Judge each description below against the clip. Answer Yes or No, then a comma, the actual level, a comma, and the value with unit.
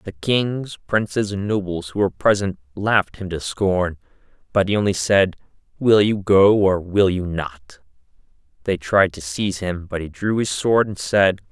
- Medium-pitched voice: No, very low, 95 Hz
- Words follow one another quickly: No, average, 180 wpm